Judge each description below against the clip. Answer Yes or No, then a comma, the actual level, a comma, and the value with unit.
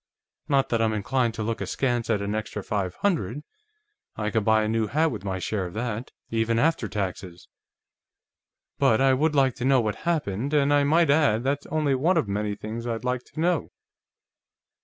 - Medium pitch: No, low, 115 Hz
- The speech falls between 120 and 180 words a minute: No, average, 195 wpm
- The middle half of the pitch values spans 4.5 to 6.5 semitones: Yes, average, 4.8 semitones